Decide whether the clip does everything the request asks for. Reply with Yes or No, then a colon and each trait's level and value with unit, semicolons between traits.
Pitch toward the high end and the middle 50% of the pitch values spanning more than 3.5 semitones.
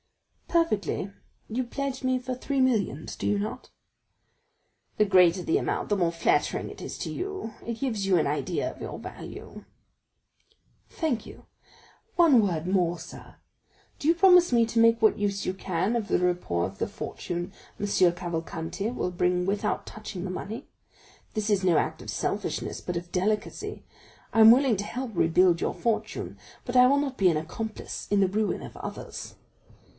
Yes: high, 205 Hz; average, 5.1 semitones